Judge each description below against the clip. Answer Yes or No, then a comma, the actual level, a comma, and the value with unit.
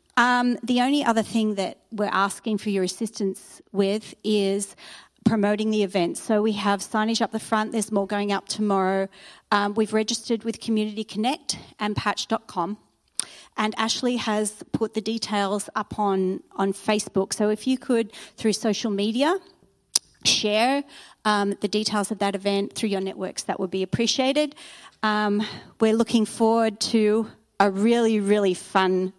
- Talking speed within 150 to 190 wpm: Yes, average, 160 wpm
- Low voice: No, high, 215 Hz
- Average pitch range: No, narrow, 2.1 semitones